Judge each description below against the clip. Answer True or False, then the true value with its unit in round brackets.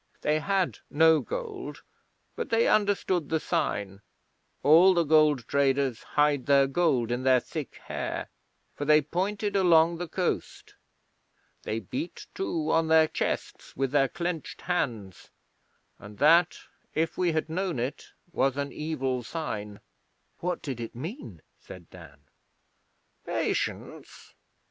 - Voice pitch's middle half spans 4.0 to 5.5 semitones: True (5.2 semitones)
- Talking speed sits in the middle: False (130 wpm)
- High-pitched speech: False (155 Hz)